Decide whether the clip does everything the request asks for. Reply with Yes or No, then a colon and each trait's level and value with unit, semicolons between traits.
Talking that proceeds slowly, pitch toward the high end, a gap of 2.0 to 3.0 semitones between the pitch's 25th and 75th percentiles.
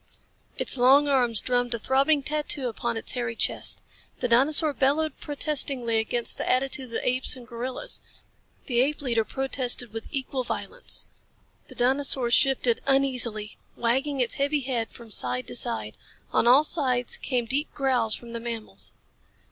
No: average, 155 wpm; very high, 255 Hz; average, 2.7 semitones